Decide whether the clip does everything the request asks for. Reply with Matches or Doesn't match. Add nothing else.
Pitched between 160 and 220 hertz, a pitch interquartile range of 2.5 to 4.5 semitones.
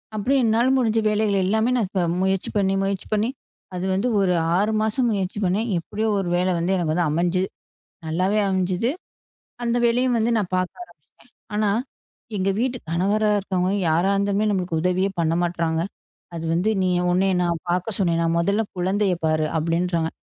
Matches